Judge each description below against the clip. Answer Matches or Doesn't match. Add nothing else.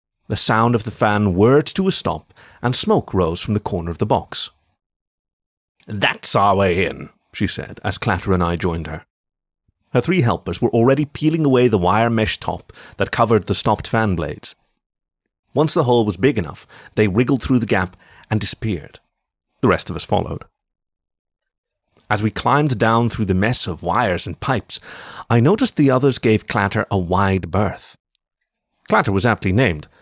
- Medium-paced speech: Matches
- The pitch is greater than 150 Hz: Doesn't match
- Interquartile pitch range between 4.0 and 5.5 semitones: Matches